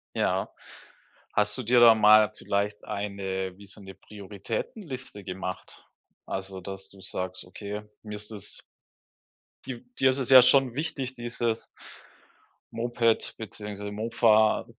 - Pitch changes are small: No, average, 3.0 semitones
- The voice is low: Yes, low, 105 Hz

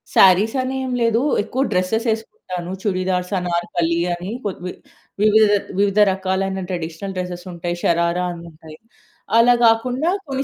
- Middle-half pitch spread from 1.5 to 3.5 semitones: No, average, 4.2 semitones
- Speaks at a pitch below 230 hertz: Yes, high, 190 Hz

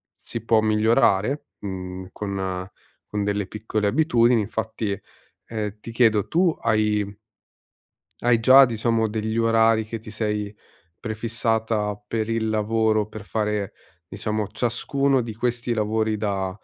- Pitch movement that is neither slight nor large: No, narrow, 1.7 semitones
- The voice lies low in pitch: Yes, low, 110 Hz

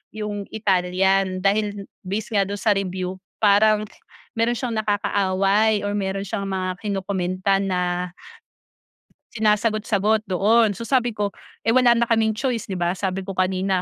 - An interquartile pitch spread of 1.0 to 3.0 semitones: Yes, narrow, 2.4 semitones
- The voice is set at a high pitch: Yes, high, 200 Hz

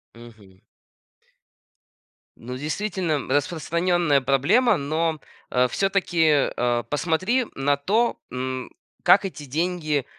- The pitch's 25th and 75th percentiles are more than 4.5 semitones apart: Yes, wide, 5.5 semitones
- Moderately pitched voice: Yes, medium, 150 Hz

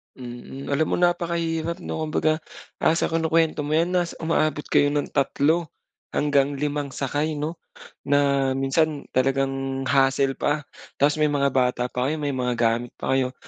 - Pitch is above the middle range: No, medium, 145 Hz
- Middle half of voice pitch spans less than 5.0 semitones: Yes, average, 2.7 semitones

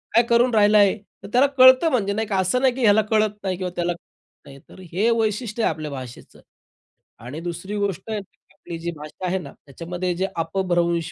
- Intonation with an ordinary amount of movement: Yes, average, 4.1 semitones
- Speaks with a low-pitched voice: No, high, 190 Hz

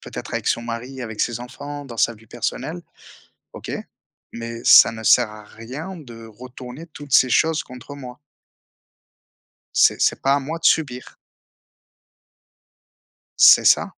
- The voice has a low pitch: Yes, low, 125 Hz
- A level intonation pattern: No, average, 3.6 semitones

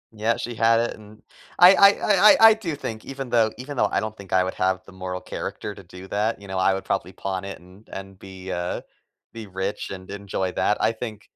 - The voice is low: Yes, low, 100 Hz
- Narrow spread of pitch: No, average, 3.3 semitones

